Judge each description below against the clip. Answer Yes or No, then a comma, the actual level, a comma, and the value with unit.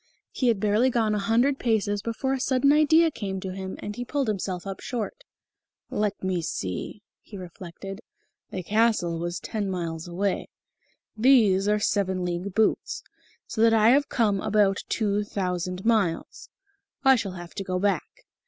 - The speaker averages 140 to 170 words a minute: Yes, average, 165 wpm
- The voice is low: No, high, 205 Hz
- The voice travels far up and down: No, average, 3.7 semitones